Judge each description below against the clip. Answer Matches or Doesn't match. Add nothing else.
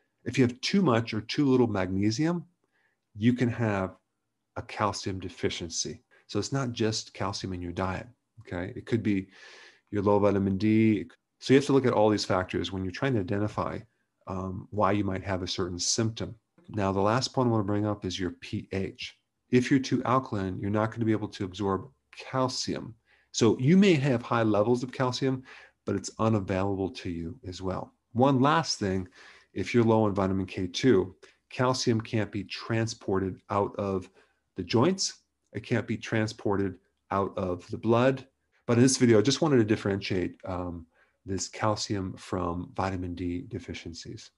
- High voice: Doesn't match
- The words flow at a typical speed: Matches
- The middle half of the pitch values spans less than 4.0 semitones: Doesn't match